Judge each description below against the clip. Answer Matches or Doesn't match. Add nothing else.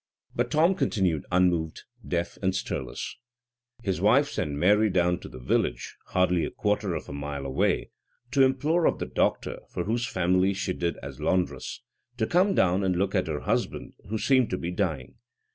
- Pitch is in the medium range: Doesn't match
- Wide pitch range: Doesn't match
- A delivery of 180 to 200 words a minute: Matches